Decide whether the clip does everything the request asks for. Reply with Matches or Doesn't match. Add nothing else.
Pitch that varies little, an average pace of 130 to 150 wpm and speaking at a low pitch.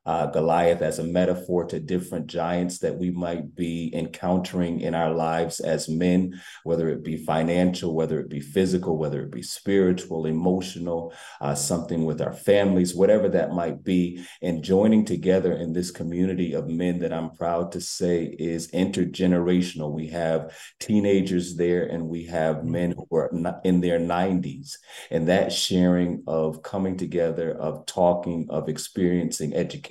Doesn't match